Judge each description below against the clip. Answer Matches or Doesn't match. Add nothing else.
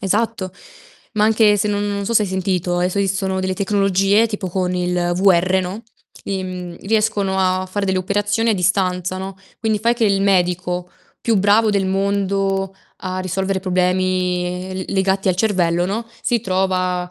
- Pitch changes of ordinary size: Doesn't match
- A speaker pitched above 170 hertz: Matches